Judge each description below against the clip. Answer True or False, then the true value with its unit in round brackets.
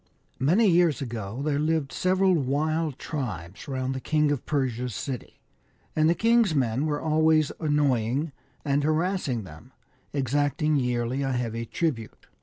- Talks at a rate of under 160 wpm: True (140 wpm)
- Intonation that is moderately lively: True (3.9 semitones)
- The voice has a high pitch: False (145 Hz)